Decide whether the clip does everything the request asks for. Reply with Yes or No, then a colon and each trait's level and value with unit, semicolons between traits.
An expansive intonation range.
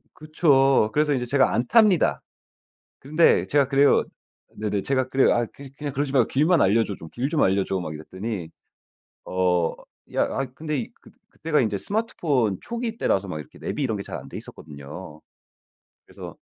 Yes: wide, 7.4 semitones